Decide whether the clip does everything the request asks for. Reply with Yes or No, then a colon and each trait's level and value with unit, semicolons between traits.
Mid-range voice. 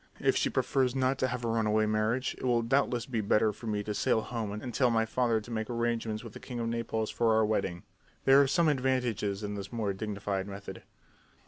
No: low, 115 Hz